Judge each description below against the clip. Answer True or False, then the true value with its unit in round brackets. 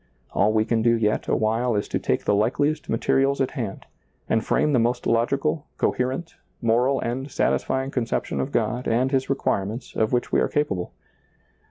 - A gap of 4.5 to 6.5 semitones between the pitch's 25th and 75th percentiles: False (3.3 semitones)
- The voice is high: False (120 Hz)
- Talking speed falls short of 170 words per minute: False (185 wpm)